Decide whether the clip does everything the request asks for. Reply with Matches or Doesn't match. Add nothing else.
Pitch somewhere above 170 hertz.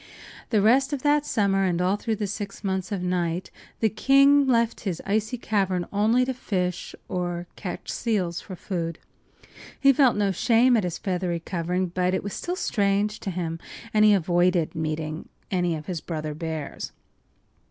Matches